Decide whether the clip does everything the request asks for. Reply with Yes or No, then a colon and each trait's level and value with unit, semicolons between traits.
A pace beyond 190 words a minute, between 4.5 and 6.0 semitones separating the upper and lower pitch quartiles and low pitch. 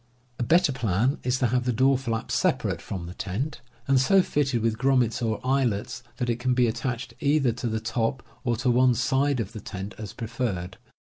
No: fast, 205 wpm; average, 2.8 semitones; low, 120 Hz